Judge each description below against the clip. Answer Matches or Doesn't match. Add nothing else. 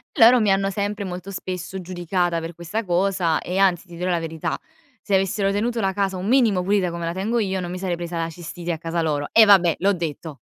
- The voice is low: Doesn't match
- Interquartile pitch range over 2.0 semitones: Matches